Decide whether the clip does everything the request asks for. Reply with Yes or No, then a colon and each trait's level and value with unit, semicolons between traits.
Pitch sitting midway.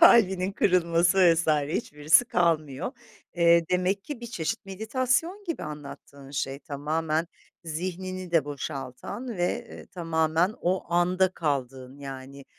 Yes: medium, 170 Hz